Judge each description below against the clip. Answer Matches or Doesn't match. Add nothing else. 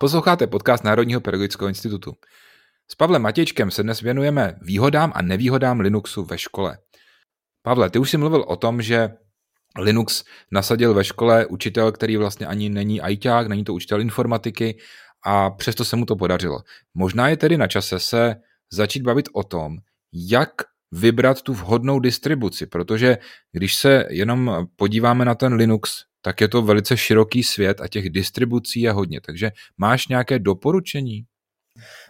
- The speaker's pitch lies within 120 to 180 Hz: Doesn't match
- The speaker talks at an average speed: Matches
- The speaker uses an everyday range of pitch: Matches